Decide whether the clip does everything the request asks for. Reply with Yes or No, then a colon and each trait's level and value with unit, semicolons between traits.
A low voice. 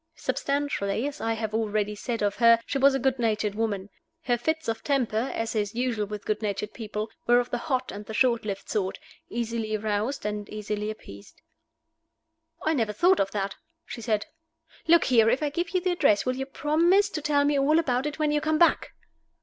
No: high, 230 Hz